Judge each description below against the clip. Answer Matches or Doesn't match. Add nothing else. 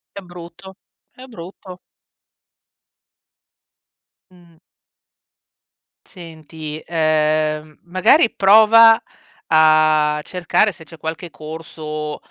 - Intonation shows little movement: Doesn't match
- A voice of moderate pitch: Matches